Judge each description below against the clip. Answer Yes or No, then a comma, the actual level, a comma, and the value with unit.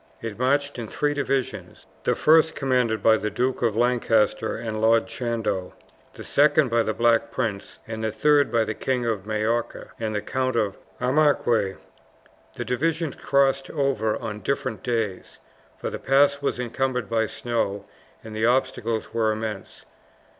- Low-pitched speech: Yes, low, 115 Hz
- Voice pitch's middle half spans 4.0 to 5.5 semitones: No, average, 3.3 semitones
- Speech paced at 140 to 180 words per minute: Yes, average, 155 wpm